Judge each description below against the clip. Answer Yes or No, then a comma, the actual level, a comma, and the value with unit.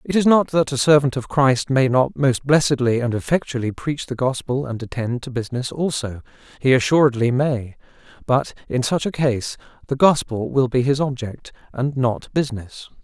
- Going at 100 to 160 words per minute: No, average, 180 wpm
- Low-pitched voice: Yes, low, 130 Hz